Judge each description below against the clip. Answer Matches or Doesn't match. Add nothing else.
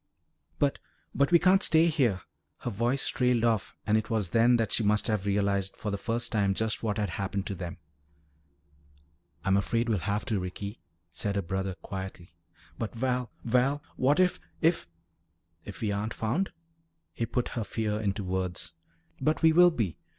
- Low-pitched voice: Matches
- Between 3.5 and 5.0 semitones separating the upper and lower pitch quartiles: Matches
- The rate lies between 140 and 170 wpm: Doesn't match